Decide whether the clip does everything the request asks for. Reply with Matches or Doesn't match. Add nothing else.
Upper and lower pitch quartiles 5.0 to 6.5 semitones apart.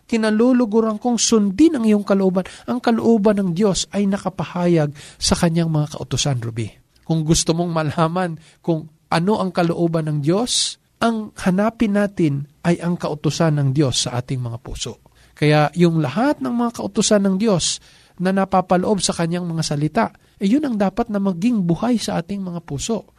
Matches